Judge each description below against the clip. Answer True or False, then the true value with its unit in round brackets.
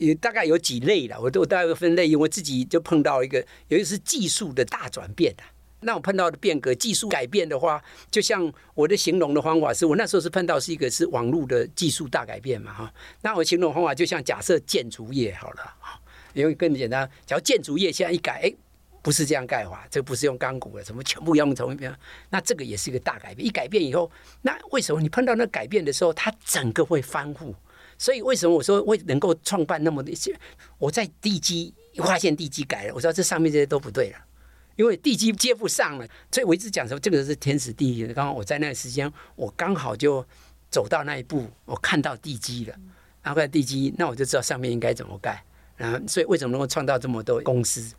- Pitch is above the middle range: False (155 Hz)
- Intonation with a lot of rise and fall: False (4.8 semitones)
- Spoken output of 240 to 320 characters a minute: False (350 characters per minute)